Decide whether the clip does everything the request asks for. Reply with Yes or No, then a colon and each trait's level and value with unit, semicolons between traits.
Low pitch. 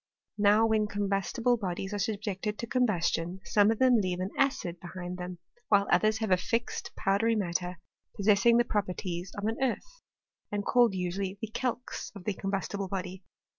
No: high, 200 Hz